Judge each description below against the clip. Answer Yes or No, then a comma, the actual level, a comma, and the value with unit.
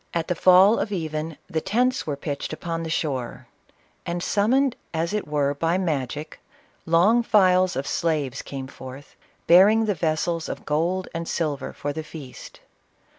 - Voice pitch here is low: No, medium, 165 Hz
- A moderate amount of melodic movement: Yes, average, 3.9 semitones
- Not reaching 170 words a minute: Yes, average, 160 wpm